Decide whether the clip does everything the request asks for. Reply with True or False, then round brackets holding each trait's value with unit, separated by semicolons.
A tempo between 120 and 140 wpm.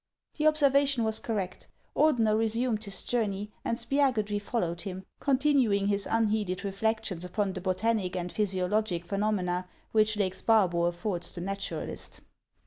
True (135 wpm)